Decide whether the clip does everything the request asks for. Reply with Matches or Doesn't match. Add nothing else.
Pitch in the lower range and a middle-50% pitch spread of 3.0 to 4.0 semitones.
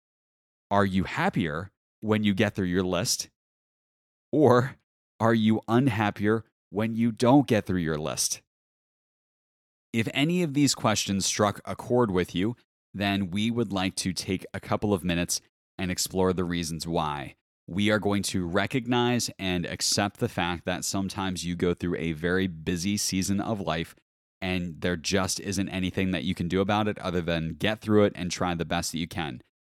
Matches